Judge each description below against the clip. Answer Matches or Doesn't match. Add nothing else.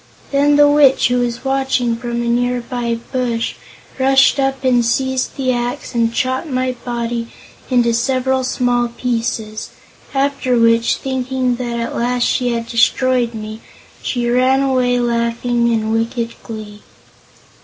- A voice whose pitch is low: Doesn't match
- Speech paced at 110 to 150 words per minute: Matches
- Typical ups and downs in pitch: Doesn't match